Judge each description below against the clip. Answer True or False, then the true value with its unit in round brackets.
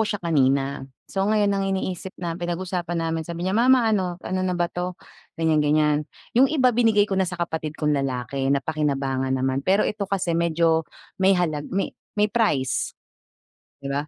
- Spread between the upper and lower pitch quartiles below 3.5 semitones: False (4.6 semitones)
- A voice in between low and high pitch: True (170 Hz)